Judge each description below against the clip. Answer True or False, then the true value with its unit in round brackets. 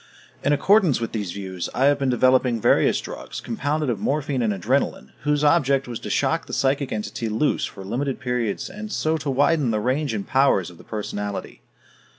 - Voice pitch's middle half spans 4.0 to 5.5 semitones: True (4.9 semitones)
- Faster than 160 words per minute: True (190 wpm)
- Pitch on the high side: False (130 Hz)